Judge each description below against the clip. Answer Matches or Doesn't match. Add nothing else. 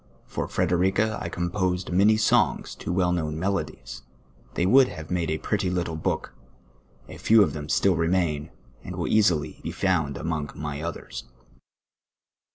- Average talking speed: Matches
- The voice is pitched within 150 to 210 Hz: Doesn't match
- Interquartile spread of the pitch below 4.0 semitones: Matches